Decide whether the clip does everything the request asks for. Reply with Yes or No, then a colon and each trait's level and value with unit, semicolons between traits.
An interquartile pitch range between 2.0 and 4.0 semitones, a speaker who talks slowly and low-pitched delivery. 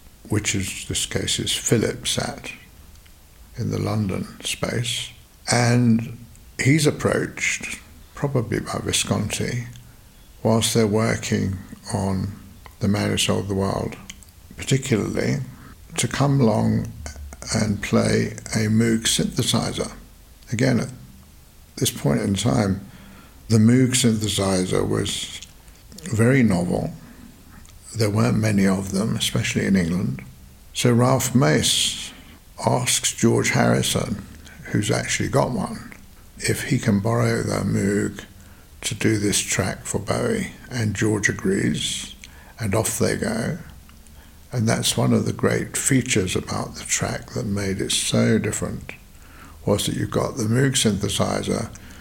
Yes: average, 3.6 semitones; slow, 125 wpm; low, 105 Hz